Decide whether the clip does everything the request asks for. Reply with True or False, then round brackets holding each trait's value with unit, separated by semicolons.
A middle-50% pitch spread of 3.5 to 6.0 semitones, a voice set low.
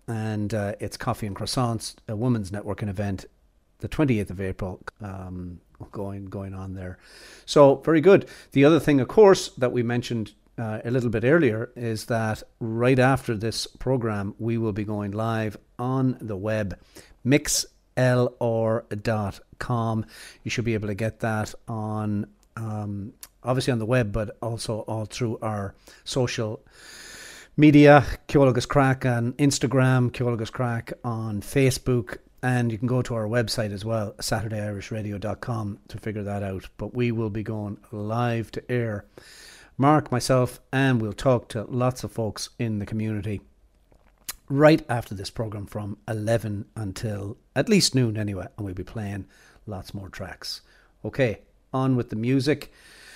False (3.1 semitones; 115 Hz)